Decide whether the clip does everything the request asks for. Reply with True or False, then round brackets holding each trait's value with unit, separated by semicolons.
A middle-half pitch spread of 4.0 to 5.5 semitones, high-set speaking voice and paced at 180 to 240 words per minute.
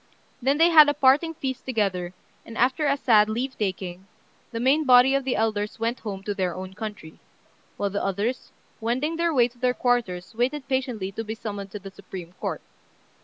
True (4.8 semitones; 230 Hz; 195 wpm)